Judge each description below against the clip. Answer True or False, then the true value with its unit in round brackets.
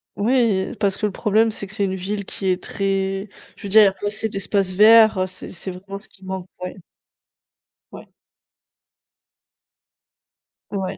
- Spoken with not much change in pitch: True (1.9 semitones)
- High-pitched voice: True (195 Hz)